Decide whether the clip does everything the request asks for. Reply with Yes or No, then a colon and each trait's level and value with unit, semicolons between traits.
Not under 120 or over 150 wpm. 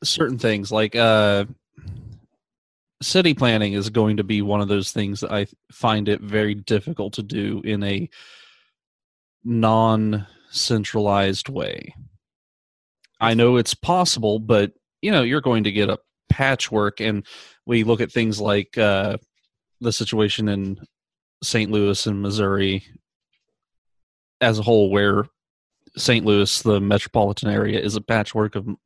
Yes: average, 140 wpm